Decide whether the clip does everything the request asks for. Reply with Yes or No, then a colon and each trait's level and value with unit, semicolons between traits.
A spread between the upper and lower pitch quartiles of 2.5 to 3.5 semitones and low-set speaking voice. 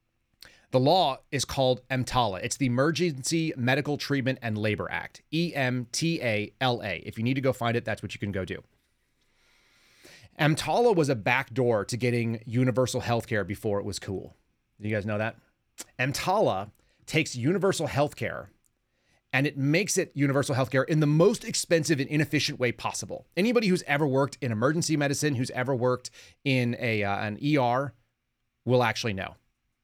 No: average, 3.9 semitones; low, 125 Hz